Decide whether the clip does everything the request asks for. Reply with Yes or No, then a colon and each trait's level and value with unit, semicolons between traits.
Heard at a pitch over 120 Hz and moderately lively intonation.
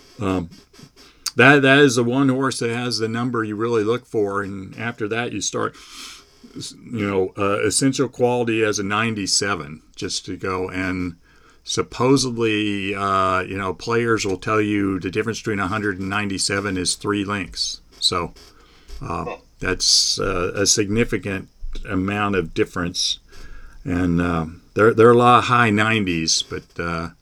No: low, 105 Hz; average, 3.8 semitones